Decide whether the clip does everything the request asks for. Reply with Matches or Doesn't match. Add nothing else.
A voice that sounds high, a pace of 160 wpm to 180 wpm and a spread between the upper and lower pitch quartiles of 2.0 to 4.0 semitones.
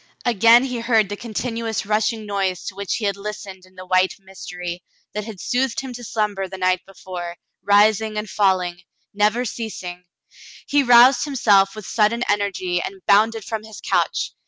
Matches